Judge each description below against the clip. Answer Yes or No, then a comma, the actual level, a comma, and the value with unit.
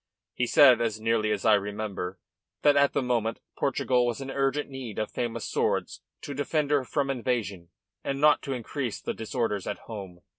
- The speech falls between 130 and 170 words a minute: No, average, 185 wpm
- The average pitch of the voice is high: No, low, 120 Hz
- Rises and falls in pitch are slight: No, average, 4.2 semitones